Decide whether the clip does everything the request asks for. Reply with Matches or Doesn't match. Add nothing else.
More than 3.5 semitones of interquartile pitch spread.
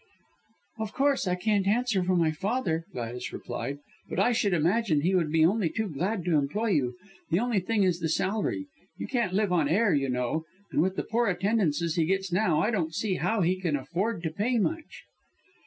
Matches